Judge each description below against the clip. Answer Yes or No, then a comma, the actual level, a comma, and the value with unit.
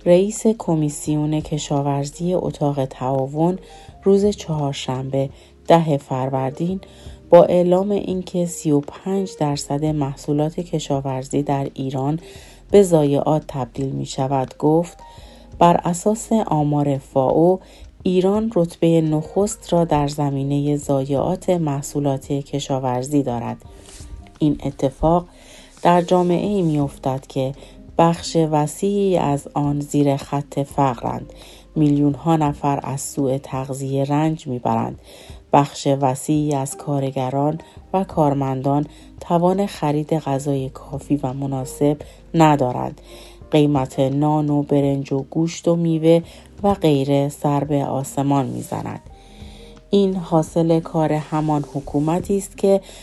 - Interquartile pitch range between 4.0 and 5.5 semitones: No, average, 3.4 semitones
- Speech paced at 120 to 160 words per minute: No, slow, 105 wpm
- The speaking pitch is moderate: Yes, medium, 145 Hz